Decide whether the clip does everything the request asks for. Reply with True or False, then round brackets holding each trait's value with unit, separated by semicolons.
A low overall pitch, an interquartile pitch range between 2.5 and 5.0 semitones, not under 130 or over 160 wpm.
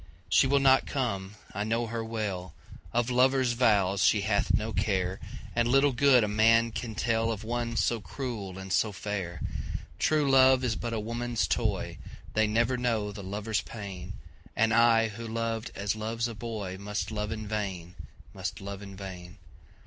True (110 Hz; 2.9 semitones; 155 wpm)